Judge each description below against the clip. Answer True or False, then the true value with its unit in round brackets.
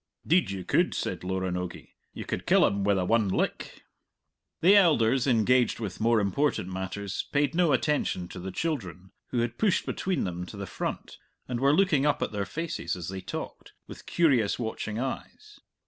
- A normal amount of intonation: False (7.5 semitones)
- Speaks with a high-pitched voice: False (115 Hz)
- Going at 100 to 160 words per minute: False (180 wpm)